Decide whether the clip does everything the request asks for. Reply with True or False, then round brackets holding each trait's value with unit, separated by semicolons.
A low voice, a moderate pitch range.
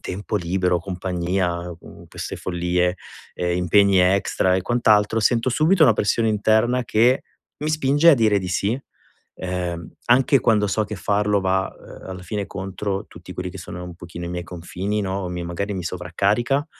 True (95 Hz; 3.3 semitones)